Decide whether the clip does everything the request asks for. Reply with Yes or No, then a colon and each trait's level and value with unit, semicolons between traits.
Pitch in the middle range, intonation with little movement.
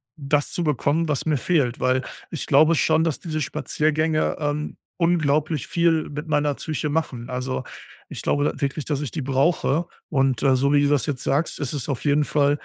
Yes: medium, 145 Hz; narrow, 2.2 semitones